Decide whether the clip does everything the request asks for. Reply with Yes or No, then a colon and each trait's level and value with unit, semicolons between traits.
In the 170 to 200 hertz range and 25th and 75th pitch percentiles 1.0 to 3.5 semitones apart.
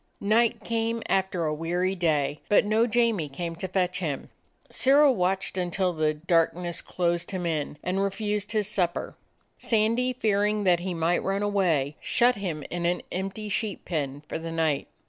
No: medium, 185 Hz; average, 3.9 semitones